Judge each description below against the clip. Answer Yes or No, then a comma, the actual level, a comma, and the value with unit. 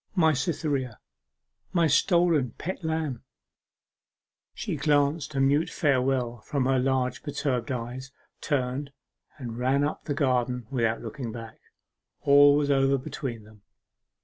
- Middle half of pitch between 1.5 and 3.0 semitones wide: Yes, narrow, 2.6 semitones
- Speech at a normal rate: No, slow, 125 wpm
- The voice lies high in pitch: No, low, 135 Hz